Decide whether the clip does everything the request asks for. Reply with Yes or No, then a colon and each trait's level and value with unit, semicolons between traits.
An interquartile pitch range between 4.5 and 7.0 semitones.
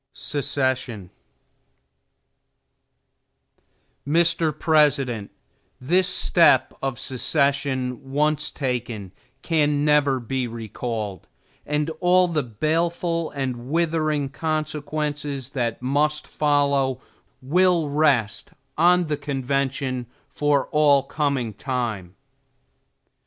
No: average, 3.2 semitones